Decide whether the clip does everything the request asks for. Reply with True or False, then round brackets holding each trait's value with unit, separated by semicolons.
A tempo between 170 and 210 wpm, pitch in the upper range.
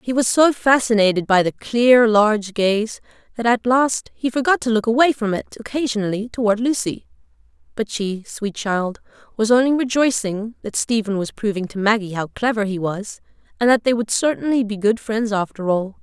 True (185 wpm; 225 Hz)